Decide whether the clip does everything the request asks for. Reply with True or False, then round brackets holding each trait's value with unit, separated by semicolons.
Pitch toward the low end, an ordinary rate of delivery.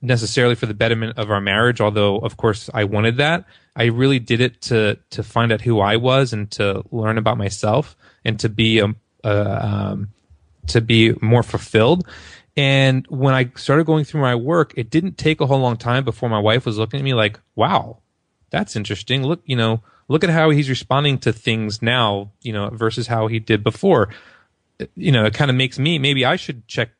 False (115 Hz; 210 wpm)